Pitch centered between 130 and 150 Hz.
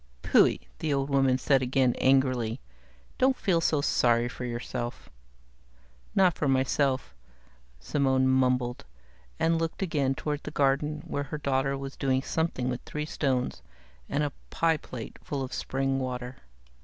Yes: low, 135 Hz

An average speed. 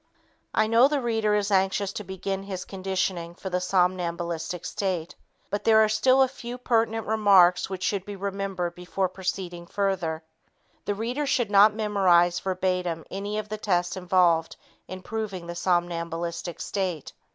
Yes: average, 155 wpm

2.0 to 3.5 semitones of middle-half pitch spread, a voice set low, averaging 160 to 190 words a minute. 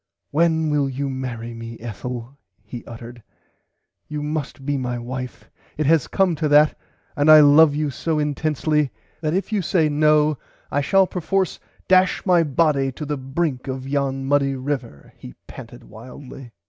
No: average, 3.1 semitones; medium, 145 Hz; average, 165 wpm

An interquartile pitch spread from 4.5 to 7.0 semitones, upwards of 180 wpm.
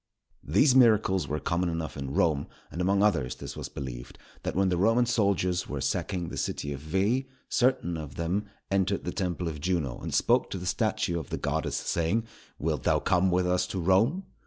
No: average, 3.9 semitones; average, 200 wpm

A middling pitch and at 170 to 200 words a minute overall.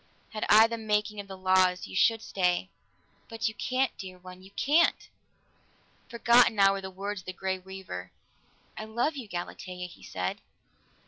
No: high, 195 Hz; average, 175 wpm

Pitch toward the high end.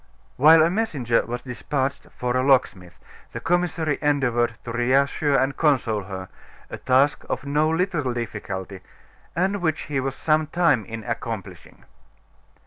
No: low, 135 Hz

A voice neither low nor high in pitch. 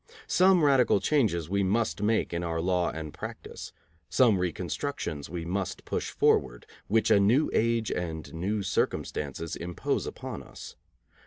No: very low, 95 Hz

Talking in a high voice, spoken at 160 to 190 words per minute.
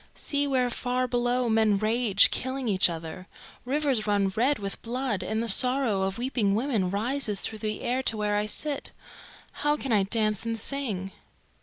Yes: high, 225 Hz; average, 175 wpm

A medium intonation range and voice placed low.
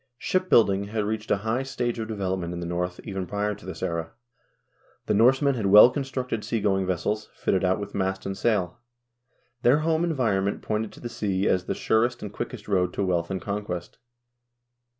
Yes: average, 3.8 semitones; low, 105 Hz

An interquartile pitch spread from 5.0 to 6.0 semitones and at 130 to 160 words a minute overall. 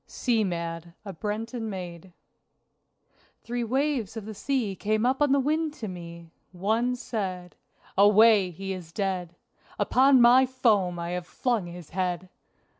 Yes: wide, 5.4 semitones; average, 145 wpm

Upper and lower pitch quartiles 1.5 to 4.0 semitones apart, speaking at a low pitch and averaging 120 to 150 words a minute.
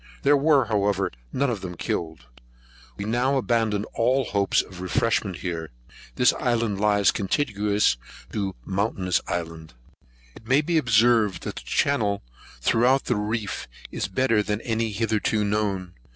Yes: average, 3.4 semitones; low, 105 Hz; average, 140 wpm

